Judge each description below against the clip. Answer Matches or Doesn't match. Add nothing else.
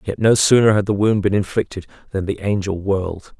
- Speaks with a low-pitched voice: Matches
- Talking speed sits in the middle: Doesn't match